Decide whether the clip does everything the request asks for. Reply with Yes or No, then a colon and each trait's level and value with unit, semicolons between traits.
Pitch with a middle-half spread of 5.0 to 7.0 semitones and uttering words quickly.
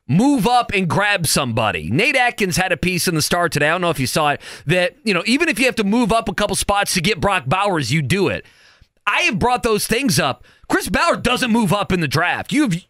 Yes: wide, 5.4 semitones; fast, 260 wpm